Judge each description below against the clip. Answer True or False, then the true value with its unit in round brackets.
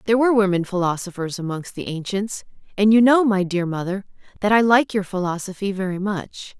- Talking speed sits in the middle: True (180 wpm)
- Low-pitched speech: False (200 Hz)